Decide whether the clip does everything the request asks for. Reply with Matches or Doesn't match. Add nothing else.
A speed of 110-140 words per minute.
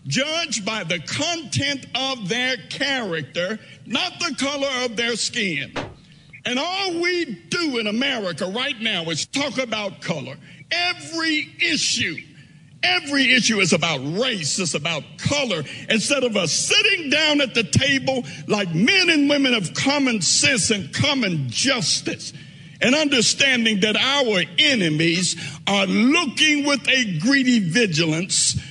Matches